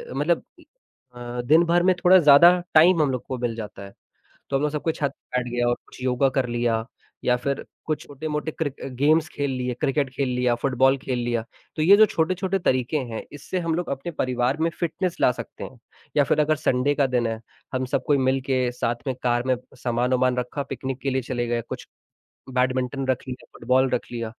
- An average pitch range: Yes, average, 3.5 semitones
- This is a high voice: No, low, 130 Hz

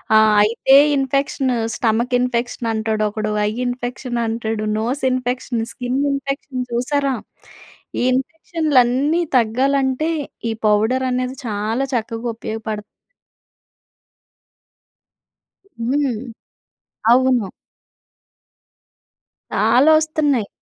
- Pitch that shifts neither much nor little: Yes, average, 3.2 semitones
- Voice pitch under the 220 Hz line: No, very high, 250 Hz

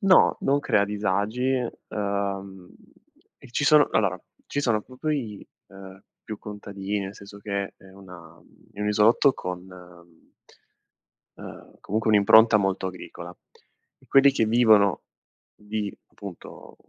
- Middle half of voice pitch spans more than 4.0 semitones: No, narrow, 2.5 semitones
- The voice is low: Yes, low, 105 Hz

